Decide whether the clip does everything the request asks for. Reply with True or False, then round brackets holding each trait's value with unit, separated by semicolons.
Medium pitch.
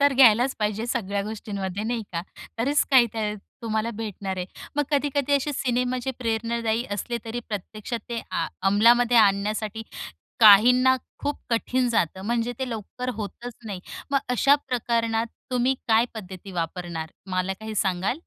False (225 Hz)